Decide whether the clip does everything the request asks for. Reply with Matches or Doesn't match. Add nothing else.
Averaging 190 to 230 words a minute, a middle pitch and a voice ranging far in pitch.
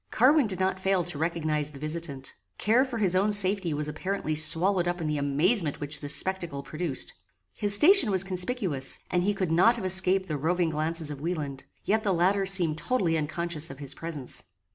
Doesn't match